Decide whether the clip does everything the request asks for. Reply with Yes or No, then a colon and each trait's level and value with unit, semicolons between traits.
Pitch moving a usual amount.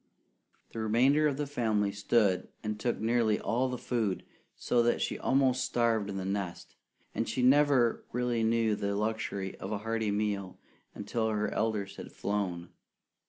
Yes: average, 3.0 semitones